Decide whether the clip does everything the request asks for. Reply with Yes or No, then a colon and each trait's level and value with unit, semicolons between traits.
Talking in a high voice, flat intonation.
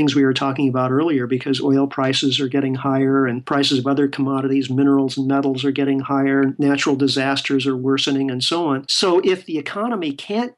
No: medium, 140 Hz; narrow, 0.9 semitones